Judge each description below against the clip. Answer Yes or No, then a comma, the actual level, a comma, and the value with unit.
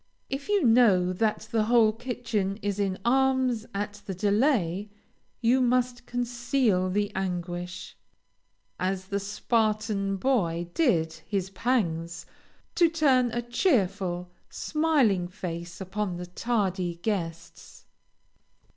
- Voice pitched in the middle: No, high, 205 Hz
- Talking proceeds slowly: Yes, slow, 110 wpm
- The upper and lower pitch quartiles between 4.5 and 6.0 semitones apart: Yes, average, 4.9 semitones